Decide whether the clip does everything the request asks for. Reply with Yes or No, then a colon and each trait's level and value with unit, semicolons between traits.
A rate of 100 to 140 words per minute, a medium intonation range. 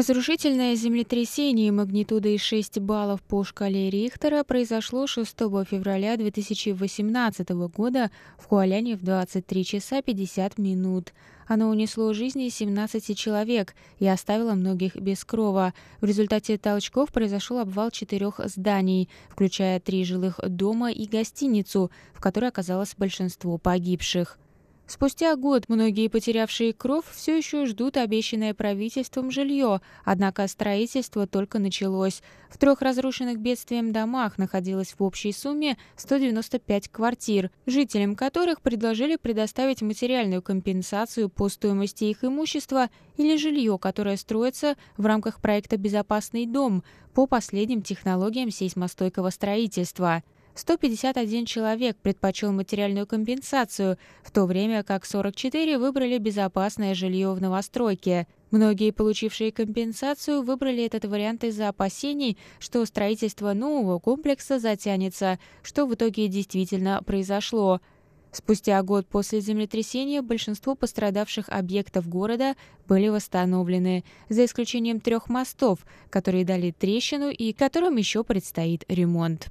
Yes: average, 115 wpm; average, 3.7 semitones